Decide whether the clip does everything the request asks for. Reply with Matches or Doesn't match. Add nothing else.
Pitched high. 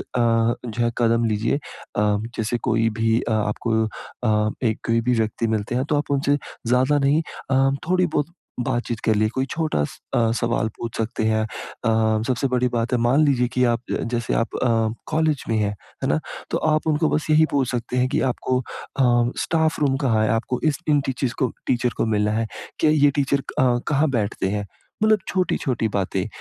Doesn't match